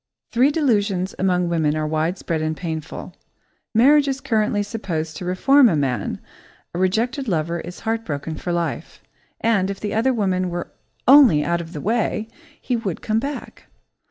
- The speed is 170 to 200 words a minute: No, average, 160 wpm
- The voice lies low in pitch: No, high, 190 Hz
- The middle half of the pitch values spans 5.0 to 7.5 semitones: Yes, wide, 5.5 semitones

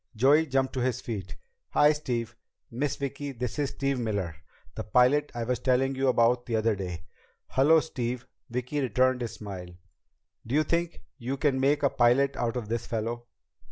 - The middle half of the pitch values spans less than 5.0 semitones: Yes, average, 3.0 semitones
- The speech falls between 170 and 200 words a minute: Yes, average, 180 wpm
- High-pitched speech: No, low, 125 Hz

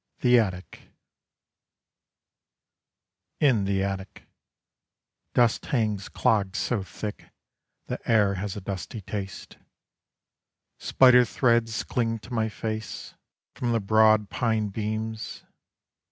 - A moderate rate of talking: No, slow, 100 wpm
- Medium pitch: No, low, 110 Hz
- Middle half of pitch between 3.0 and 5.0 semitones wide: No, narrow, 2.5 semitones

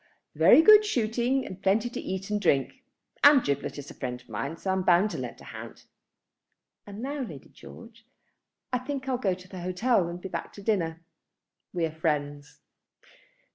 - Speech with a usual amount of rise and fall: No, wide, 6.7 semitones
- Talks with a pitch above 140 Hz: Yes, high, 190 Hz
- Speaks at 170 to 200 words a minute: Yes, average, 185 wpm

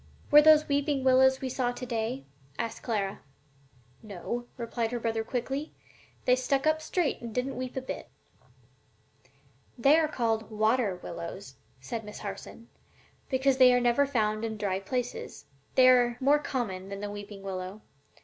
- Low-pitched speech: No, high, 240 Hz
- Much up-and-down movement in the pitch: No, average, 3.7 semitones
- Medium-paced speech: Yes, average, 170 wpm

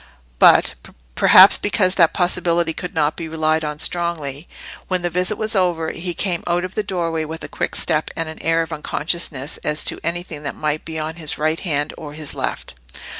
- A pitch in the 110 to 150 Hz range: No, medium, 165 Hz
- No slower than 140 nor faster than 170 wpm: No, average, 190 wpm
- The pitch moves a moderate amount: No, narrow, 2.3 semitones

